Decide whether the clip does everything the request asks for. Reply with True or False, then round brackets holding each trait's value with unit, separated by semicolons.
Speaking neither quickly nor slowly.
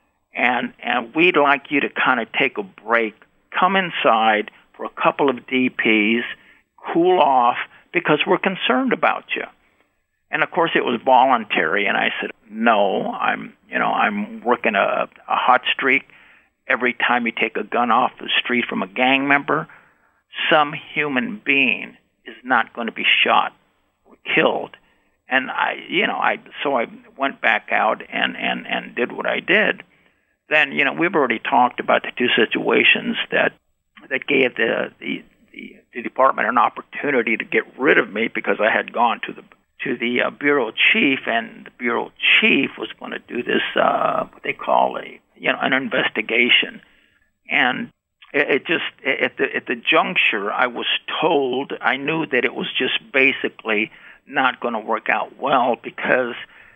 True (175 wpm)